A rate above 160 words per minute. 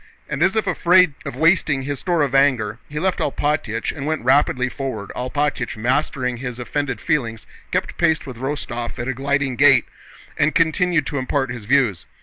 Yes: average, 175 wpm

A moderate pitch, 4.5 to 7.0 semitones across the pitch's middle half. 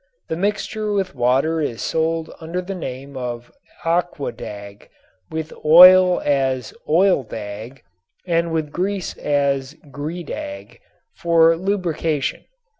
Yes: medium, 160 Hz; average, 4.9 semitones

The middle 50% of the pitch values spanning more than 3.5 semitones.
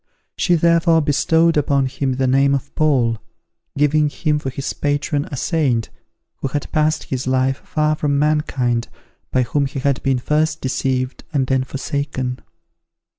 No: narrow, 2.6 semitones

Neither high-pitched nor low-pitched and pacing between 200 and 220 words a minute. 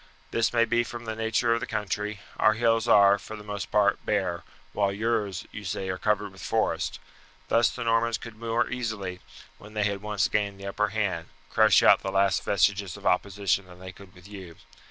No: low, 105 Hz; fast, 205 wpm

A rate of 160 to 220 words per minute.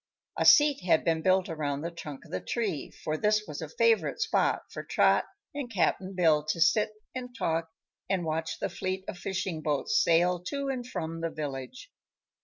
Yes: average, 190 wpm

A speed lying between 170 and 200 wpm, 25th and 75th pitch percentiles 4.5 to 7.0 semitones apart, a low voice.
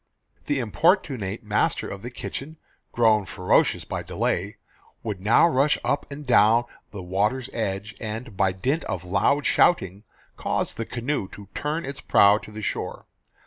No: average, 155 wpm; average, 5.2 semitones; low, 110 Hz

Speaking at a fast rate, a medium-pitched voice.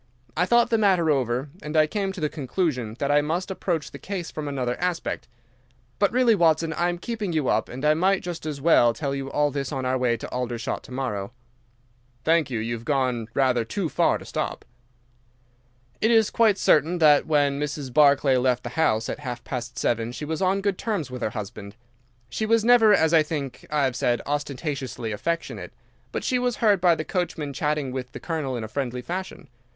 Yes: fast, 210 wpm; medium, 150 Hz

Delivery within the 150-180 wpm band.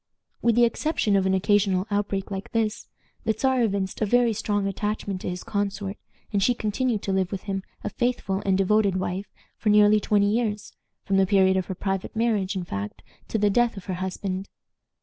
No: average, 200 wpm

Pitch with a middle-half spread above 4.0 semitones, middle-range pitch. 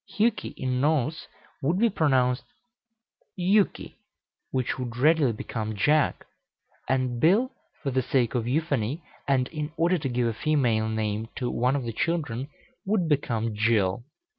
No: average, 5.2 semitones; low, 130 Hz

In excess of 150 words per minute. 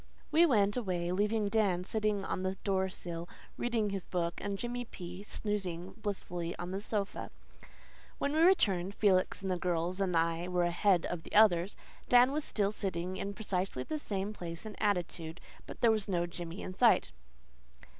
Yes: average, 175 wpm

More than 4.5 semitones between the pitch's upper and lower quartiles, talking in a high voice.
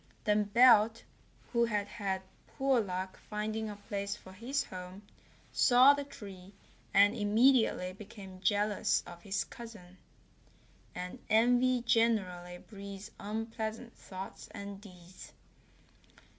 No: average, 3.3 semitones; high, 210 Hz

